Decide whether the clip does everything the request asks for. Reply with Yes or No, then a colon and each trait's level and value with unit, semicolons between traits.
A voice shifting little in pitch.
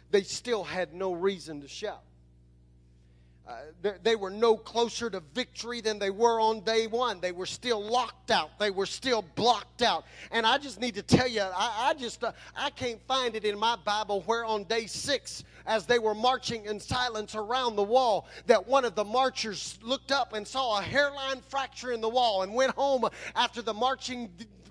No: average, 3.5 semitones